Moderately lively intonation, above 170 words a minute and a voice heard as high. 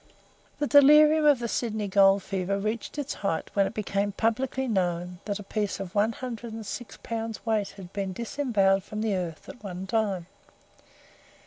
Yes: average, 3.2 semitones; average, 180 wpm; high, 210 Hz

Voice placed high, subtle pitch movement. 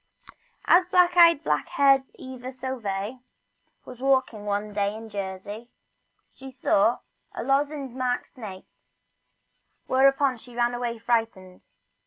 No: high, 245 Hz; average, 4.3 semitones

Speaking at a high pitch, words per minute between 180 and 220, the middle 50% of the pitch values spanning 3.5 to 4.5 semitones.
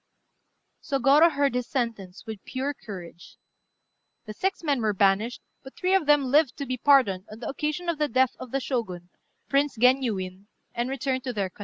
No: very high, 255 Hz; average, 185 wpm; average, 4.9 semitones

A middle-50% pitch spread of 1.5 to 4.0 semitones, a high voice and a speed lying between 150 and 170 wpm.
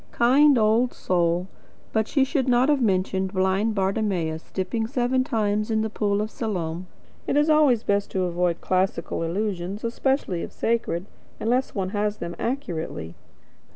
No: average, 4.6 semitones; high, 210 Hz; average, 155 wpm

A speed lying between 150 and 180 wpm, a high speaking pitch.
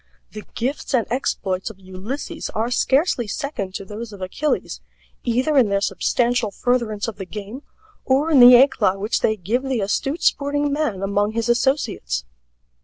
Yes: average, 165 wpm; high, 235 Hz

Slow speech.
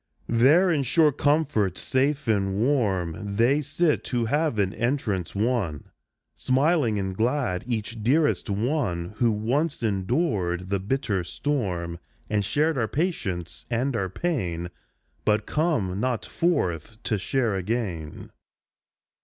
Yes: slow, 125 wpm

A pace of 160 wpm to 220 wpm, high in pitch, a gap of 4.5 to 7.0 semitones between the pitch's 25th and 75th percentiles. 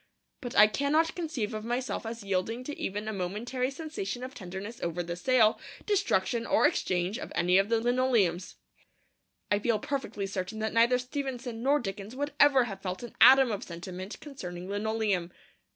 Yes: average, 170 wpm; high, 220 Hz; average, 4.9 semitones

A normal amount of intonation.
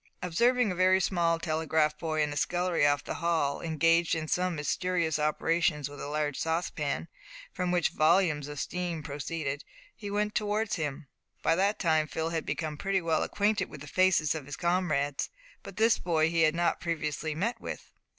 Yes: average, 3.0 semitones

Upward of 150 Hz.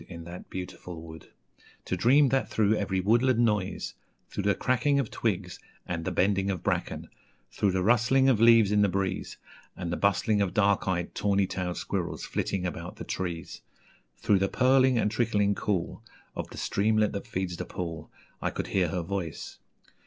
No: low, 100 Hz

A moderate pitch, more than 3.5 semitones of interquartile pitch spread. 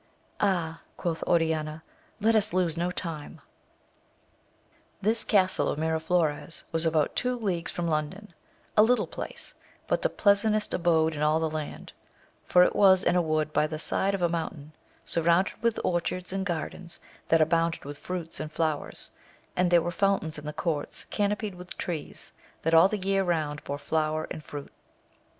No: medium, 170 Hz; average, 3.2 semitones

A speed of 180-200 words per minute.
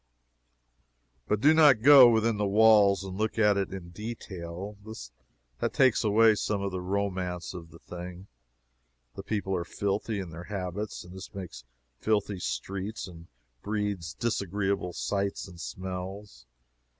No: average, 145 wpm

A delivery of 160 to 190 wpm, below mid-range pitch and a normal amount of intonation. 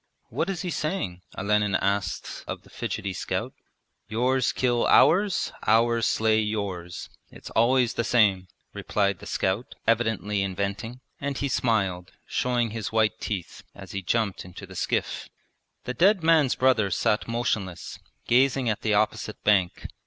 No: average, 145 wpm; low, 110 Hz; average, 4.0 semitones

